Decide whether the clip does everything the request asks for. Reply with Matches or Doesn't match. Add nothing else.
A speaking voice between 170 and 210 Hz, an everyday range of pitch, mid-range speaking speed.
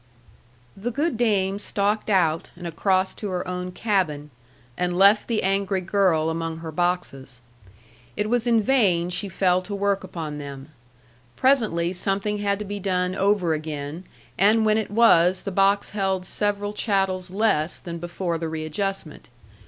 Matches